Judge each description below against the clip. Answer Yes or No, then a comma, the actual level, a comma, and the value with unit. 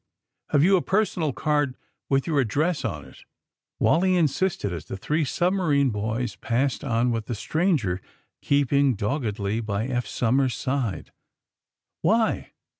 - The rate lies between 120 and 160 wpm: Yes, average, 145 wpm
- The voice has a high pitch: No, low, 135 Hz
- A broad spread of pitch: Yes, wide, 5.7 semitones